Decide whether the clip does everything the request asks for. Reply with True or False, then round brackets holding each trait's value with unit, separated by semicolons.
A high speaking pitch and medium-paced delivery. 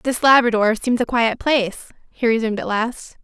True (230 Hz; 185 wpm)